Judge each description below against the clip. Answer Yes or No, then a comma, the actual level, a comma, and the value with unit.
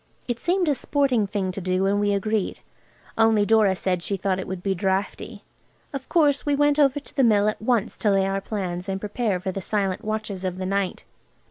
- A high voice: Yes, high, 205 Hz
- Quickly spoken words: Yes, fast, 220 wpm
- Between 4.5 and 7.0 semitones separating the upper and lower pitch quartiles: No, average, 3.4 semitones